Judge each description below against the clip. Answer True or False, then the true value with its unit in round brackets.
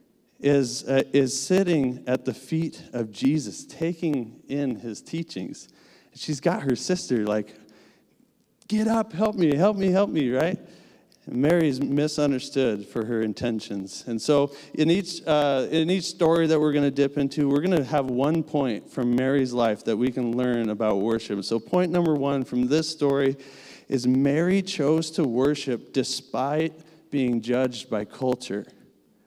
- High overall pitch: False (140 Hz)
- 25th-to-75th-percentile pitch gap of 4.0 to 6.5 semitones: True (4.4 semitones)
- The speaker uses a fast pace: False (160 wpm)